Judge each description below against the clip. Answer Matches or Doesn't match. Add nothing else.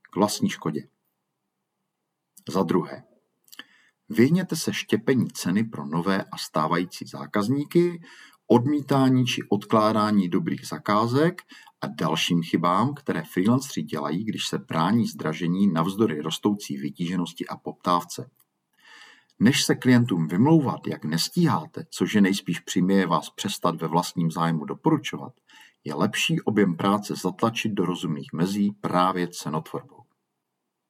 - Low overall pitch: Matches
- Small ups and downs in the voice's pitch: Doesn't match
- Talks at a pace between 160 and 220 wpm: Doesn't match